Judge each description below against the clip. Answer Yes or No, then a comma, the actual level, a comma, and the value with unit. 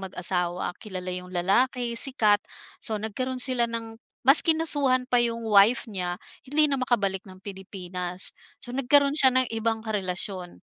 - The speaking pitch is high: Yes, high, 225 Hz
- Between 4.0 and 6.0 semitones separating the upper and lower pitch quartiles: Yes, average, 5.3 semitones